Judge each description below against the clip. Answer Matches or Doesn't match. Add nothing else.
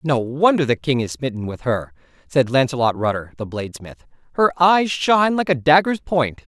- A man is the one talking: Matches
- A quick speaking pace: Doesn't match